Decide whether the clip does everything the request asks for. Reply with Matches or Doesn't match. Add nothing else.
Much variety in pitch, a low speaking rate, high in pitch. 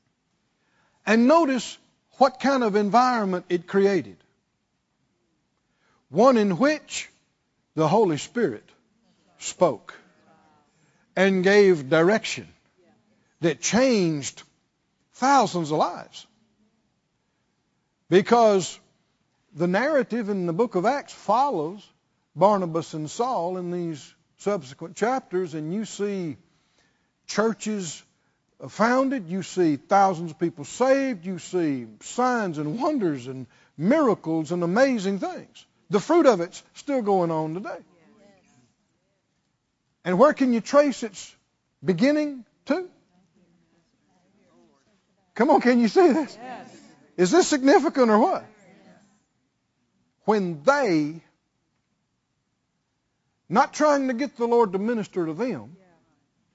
Matches